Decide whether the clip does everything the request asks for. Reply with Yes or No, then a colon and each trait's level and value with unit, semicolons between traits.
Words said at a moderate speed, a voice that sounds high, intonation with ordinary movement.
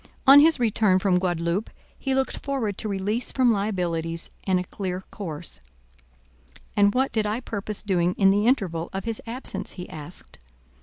Yes: average, 165 wpm; high, 200 Hz; average, 4.1 semitones